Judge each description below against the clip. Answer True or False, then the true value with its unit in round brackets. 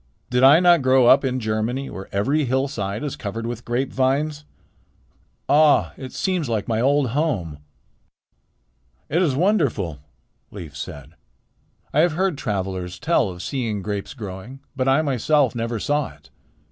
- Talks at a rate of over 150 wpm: False (145 wpm)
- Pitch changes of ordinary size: False (5.8 semitones)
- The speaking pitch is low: True (130 Hz)